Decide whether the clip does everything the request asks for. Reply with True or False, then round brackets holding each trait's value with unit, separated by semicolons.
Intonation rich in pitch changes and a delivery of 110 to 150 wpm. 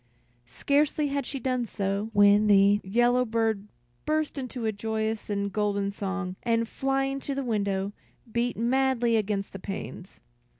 False (4.0 semitones; 145 wpm)